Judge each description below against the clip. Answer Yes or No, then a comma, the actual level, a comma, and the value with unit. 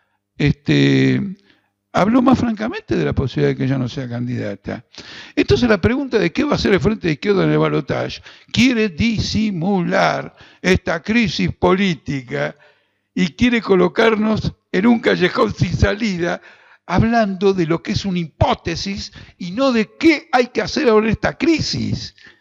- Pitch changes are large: Yes, wide, 6.9 semitones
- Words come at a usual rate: Yes, average, 160 wpm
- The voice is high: Yes, high, 195 Hz